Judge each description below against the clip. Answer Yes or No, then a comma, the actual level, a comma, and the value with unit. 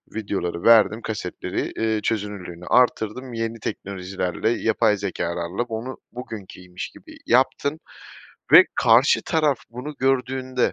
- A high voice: No, low, 110 Hz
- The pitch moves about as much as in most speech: Yes, average, 4.3 semitones